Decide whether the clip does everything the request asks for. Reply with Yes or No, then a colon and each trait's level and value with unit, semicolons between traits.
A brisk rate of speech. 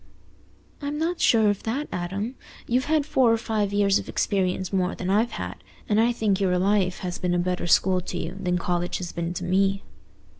Yes: fast, 215 wpm